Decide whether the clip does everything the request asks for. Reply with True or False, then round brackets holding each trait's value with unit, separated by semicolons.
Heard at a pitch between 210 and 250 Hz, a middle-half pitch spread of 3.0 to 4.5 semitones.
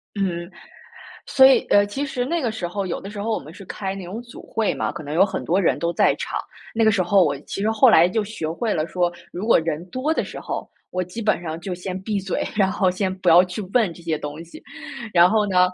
False (190 Hz; 3.8 semitones)